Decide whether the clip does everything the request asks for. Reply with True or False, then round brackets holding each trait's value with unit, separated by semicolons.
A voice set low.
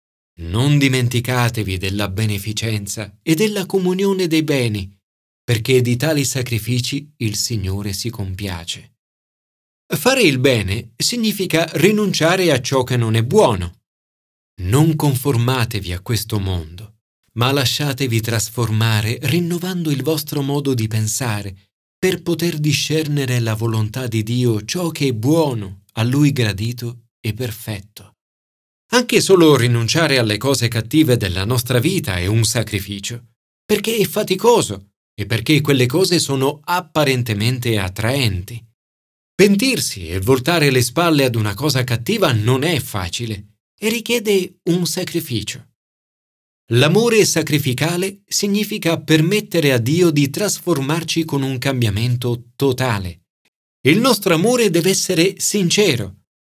True (125 Hz)